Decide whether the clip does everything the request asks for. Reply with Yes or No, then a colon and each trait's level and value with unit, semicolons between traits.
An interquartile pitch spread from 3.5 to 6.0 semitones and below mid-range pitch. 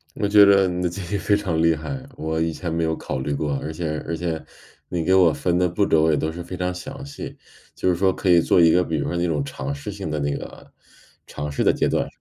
No: average, 2.8 semitones; very low, 85 Hz